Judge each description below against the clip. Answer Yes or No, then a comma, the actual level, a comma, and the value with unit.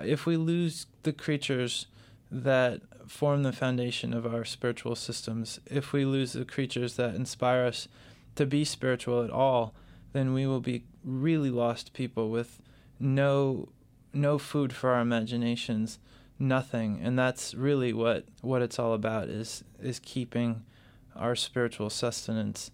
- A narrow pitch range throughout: Yes, narrow, 2.3 semitones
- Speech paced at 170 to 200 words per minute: No, average, 145 wpm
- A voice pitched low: Yes, low, 125 Hz